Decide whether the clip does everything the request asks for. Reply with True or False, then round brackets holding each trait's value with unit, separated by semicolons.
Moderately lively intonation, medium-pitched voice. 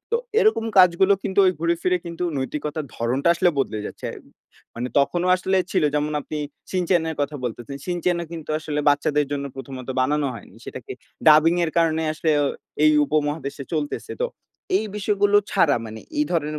True (3.7 semitones; 155 Hz)